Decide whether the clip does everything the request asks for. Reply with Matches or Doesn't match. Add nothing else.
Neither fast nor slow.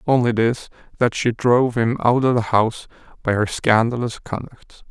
Matches